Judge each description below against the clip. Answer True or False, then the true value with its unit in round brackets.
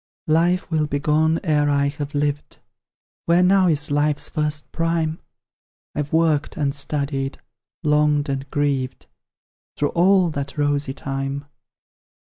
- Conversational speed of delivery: False (130 wpm)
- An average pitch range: False (1.9 semitones)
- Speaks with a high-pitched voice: False (150 Hz)